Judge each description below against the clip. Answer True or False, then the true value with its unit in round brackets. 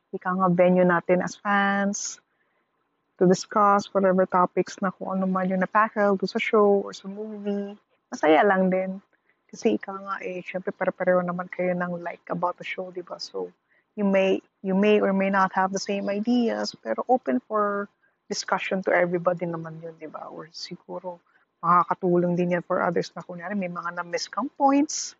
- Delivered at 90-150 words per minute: False (180 wpm)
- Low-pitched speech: False (190 Hz)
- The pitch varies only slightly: True (2.1 semitones)